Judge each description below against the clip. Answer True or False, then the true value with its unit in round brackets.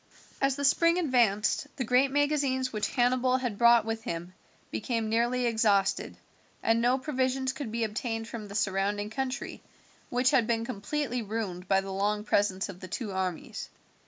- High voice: True (230 Hz)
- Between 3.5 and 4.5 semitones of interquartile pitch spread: True (4.0 semitones)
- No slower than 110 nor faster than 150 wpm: False (165 wpm)